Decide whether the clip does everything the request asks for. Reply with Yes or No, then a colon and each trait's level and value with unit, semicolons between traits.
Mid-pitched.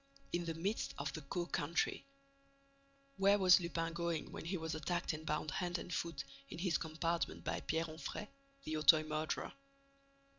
Yes: medium, 165 Hz